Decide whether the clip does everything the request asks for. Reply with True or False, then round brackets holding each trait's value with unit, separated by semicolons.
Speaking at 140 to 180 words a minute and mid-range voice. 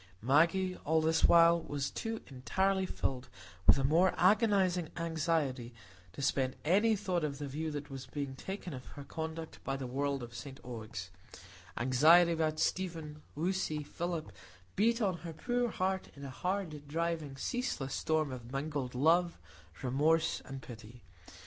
True (155 wpm; 155 Hz)